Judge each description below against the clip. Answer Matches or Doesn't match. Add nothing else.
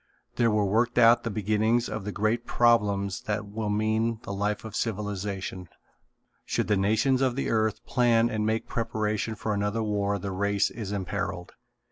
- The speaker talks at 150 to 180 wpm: Matches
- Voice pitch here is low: Matches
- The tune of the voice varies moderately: Doesn't match